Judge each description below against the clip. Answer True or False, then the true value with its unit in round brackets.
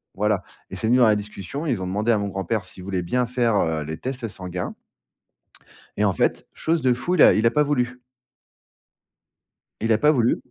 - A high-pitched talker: False (110 Hz)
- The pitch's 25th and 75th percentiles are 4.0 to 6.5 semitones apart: True (4.5 semitones)